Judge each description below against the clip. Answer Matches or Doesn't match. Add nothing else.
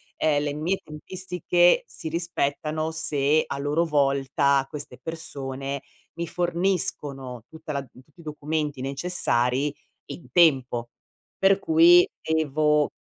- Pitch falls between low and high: Matches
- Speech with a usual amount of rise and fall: Matches